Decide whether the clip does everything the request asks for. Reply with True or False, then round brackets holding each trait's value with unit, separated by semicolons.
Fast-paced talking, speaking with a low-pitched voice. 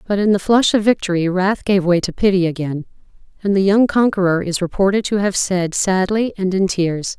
False (210 wpm; 190 Hz)